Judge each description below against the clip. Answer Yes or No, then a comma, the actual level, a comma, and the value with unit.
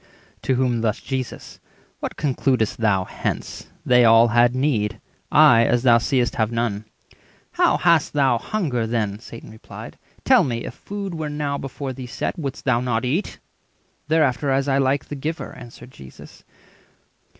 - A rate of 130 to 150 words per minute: No, average, 160 wpm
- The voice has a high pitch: No, low, 125 Hz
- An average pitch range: Yes, average, 3.3 semitones